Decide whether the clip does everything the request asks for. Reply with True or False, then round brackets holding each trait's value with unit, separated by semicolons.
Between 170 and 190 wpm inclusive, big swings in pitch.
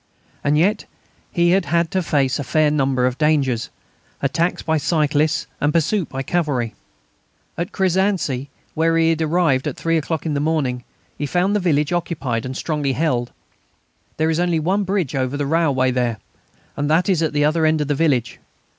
False (180 wpm; 3.6 semitones)